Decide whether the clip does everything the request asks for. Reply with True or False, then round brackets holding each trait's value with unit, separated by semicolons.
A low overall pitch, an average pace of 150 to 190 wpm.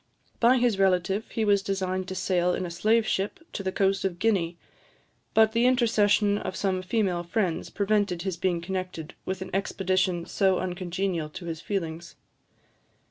False (190 Hz; 165 wpm)